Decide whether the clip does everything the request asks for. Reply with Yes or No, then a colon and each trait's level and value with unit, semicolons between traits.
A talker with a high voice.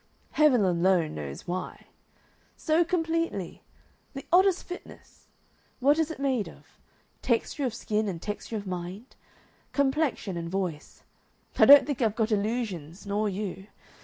Yes: high, 215 Hz